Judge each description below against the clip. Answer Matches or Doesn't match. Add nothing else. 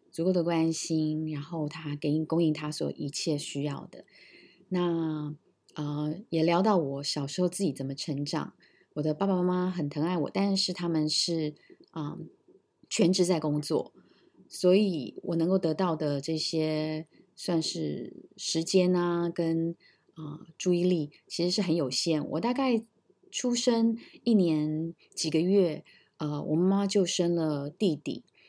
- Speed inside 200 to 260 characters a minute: Matches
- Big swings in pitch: Doesn't match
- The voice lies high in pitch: Doesn't match